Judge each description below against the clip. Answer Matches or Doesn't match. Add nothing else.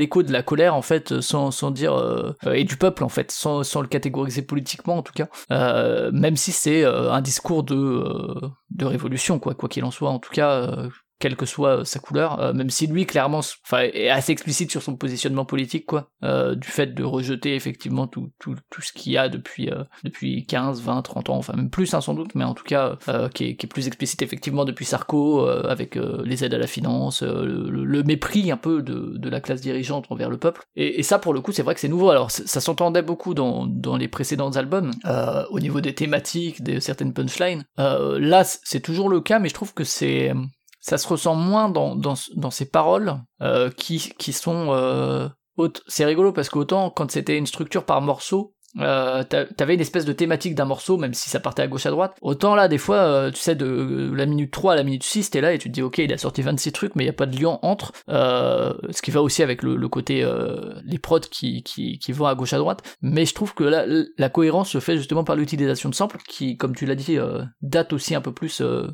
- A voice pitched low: Doesn't match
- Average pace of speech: Doesn't match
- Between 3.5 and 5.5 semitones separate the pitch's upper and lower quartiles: Matches